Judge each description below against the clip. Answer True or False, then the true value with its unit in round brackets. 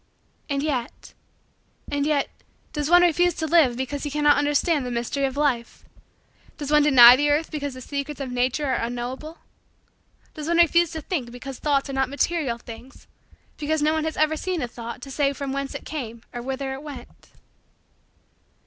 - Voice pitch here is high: True (280 Hz)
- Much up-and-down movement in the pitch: False (2.9 semitones)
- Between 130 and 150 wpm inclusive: False (185 wpm)